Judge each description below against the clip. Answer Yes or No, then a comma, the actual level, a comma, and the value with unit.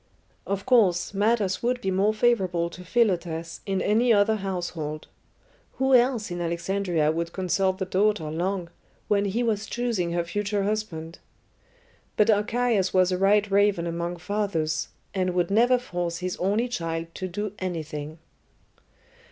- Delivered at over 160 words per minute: No, average, 145 wpm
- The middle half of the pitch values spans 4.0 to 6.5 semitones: No, average, 3.6 semitones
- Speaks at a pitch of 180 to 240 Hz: Yes, high, 190 Hz